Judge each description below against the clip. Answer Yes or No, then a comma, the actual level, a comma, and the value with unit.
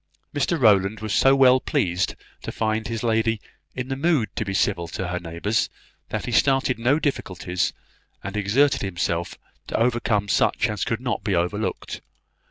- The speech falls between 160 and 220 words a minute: Yes, average, 170 wpm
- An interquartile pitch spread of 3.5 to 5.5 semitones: Yes, average, 4.5 semitones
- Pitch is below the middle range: Yes, low, 110 Hz